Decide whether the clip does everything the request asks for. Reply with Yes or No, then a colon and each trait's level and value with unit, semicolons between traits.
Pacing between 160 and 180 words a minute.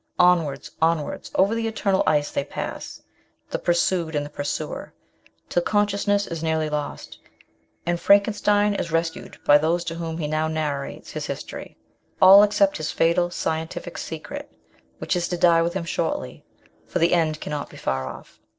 Yes: average, 165 wpm